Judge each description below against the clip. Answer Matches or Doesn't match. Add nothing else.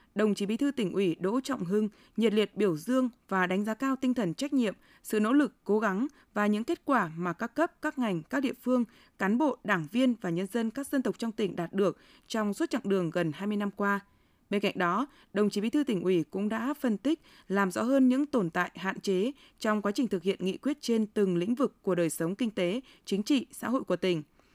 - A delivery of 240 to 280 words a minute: Matches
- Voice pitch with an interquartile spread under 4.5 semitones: Doesn't match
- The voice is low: Doesn't match